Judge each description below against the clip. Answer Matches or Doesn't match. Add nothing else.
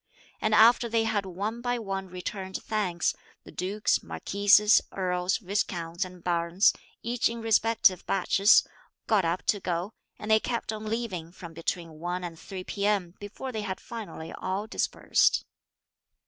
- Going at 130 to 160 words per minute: Matches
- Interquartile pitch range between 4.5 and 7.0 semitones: Doesn't match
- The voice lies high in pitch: Matches